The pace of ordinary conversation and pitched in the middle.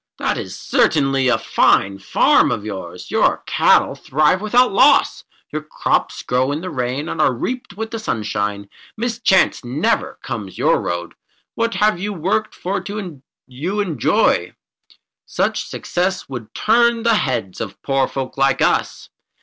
Yes: average, 150 wpm; medium, 145 Hz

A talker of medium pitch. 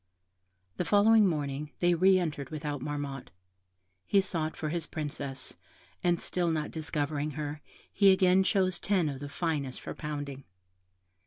Yes: medium, 155 Hz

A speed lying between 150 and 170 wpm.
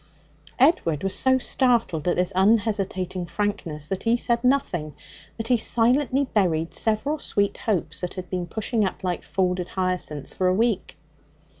Yes: average, 155 wpm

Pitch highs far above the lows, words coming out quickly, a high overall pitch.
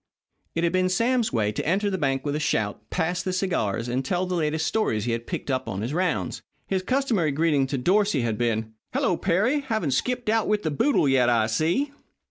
No: wide, 7.5 semitones; fast, 220 wpm; medium, 160 Hz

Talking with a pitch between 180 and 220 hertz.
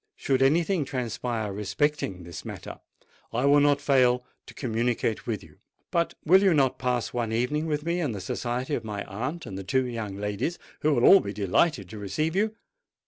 No: low, 125 Hz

